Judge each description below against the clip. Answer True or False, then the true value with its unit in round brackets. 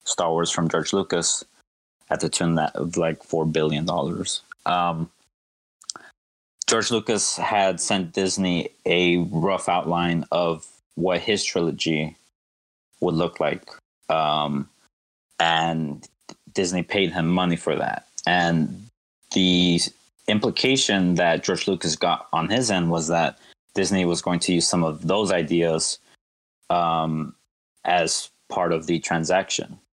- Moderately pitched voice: False (85 Hz)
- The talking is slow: True (130 wpm)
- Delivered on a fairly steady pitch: True (1.8 semitones)